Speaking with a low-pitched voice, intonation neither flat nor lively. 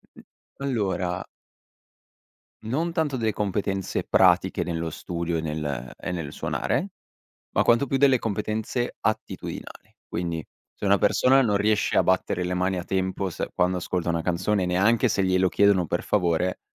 Yes: very low, 95 Hz; average, 3.6 semitones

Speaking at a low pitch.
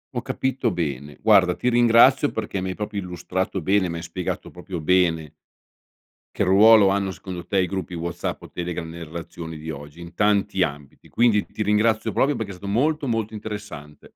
Yes: very low, 95 Hz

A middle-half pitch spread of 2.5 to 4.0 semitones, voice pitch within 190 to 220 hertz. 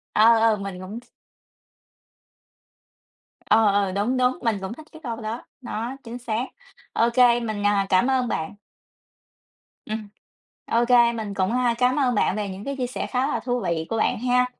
No: average, 3.3 semitones; high, 230 Hz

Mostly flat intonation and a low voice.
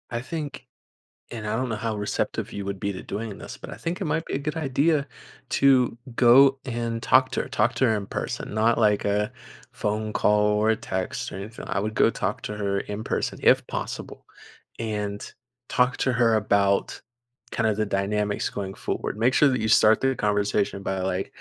No: average, 3.5 semitones; low, 110 Hz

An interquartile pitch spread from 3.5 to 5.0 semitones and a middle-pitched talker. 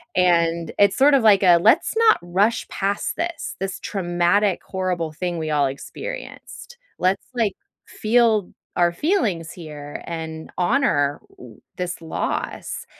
Yes: average, 4.5 semitones; medium, 180 Hz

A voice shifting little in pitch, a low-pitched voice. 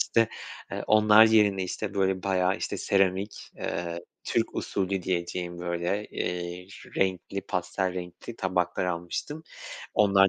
Yes: narrow, 2.1 semitones; very low, 95 Hz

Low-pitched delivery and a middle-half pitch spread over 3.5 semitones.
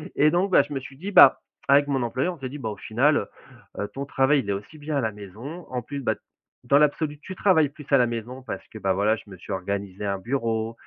Yes: low, 130 Hz; average, 5.1 semitones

